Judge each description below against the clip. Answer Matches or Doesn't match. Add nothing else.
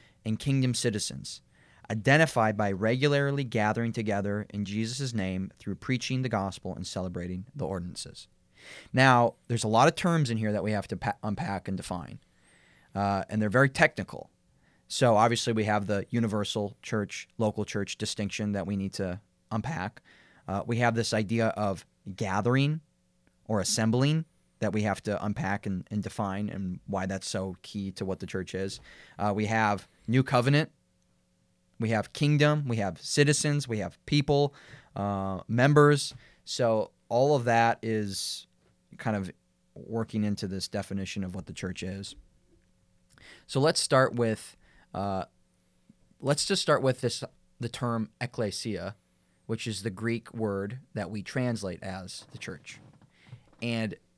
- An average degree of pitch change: Matches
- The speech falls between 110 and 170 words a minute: Matches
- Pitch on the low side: Matches